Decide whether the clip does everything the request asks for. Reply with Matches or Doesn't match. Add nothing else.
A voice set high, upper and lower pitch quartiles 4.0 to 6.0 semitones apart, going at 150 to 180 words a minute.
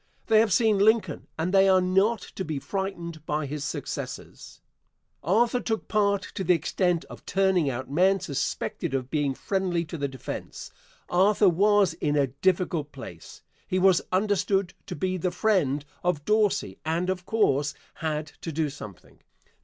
Doesn't match